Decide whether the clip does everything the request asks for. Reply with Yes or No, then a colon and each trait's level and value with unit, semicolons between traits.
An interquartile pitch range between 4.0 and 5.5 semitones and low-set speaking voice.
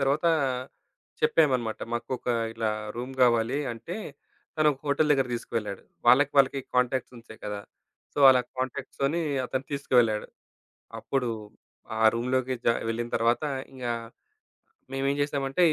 No: average, 2.8 semitones; low, 130 Hz